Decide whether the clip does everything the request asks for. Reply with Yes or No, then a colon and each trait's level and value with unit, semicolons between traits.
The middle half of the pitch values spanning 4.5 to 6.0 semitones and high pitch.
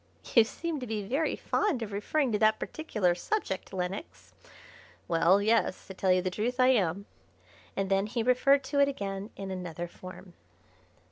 Yes: average, 5.2 semitones; high, 205 Hz